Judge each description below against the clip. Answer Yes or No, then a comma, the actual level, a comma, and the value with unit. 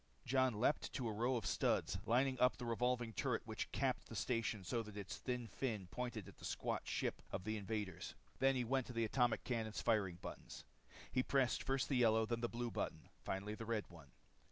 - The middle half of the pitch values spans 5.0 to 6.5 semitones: No, average, 2.7 semitones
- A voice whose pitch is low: Yes, low, 115 Hz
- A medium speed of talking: No, fast, 210 wpm